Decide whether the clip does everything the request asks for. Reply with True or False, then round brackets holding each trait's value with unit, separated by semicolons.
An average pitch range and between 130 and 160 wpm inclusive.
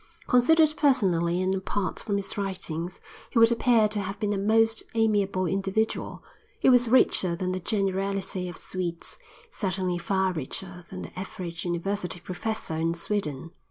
True (3.1 semitones; 155 wpm)